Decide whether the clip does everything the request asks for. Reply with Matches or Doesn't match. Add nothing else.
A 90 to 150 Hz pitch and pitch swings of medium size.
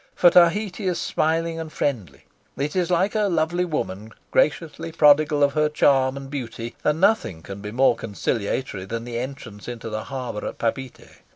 Doesn't match